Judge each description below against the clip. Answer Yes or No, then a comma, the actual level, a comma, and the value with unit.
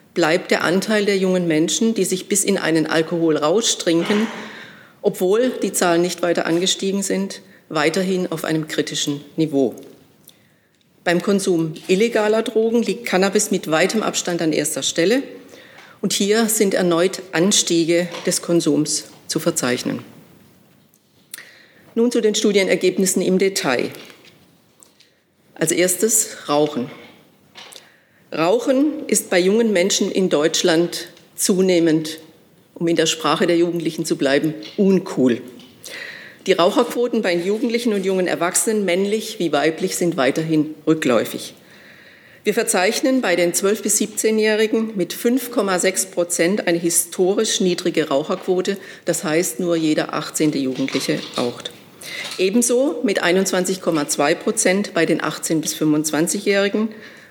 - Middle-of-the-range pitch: Yes, medium, 180 Hz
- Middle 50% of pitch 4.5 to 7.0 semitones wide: No, average, 4.1 semitones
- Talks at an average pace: No, slow, 120 wpm